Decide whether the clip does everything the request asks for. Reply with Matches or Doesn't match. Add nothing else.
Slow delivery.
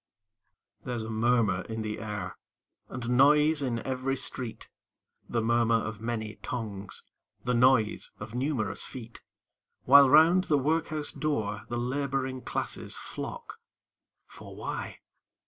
Matches